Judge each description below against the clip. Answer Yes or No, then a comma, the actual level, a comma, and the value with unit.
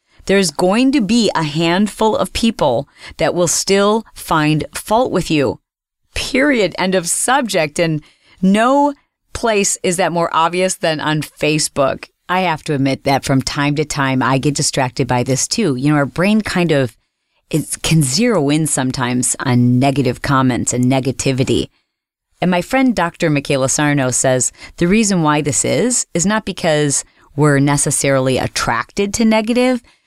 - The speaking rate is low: No, average, 160 wpm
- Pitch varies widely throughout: Yes, wide, 5.8 semitones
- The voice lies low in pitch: No, medium, 155 Hz